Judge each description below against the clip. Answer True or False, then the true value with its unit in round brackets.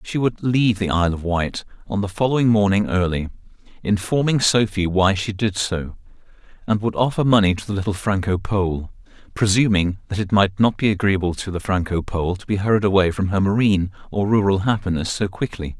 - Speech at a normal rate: True (190 wpm)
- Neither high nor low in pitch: False (100 Hz)